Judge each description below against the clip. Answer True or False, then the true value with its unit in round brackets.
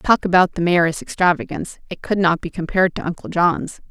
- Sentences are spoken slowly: False (200 wpm)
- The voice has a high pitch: False (180 Hz)